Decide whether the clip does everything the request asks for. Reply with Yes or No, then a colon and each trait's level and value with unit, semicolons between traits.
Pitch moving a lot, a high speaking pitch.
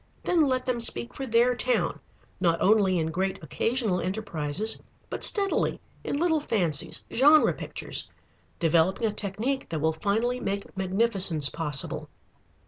Yes: wide, 6.7 semitones; high, 200 Hz